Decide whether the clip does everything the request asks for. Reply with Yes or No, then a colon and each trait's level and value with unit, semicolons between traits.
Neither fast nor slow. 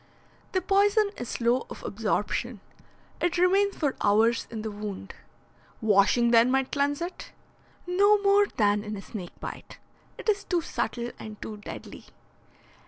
Yes: average, 150 wpm